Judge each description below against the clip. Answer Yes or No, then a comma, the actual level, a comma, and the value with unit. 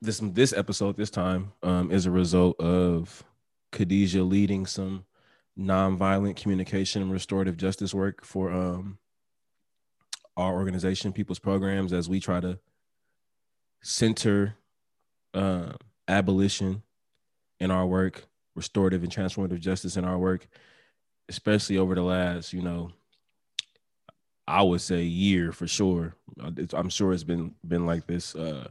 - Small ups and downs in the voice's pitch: Yes, narrow, 1.5 semitones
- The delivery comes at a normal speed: No, slow, 130 wpm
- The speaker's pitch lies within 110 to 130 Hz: No, very low, 95 Hz